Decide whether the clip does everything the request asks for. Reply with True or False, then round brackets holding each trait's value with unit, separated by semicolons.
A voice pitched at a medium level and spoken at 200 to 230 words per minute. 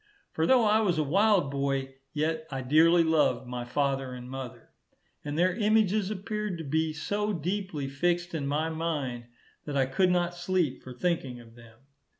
False (160 Hz; 175 wpm)